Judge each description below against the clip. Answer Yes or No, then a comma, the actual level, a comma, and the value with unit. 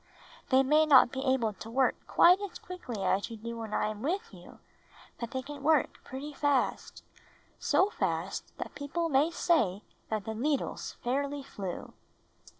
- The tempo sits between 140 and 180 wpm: Yes, average, 170 wpm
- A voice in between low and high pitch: No, very high, 265 Hz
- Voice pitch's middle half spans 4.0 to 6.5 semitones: Yes, average, 5.0 semitones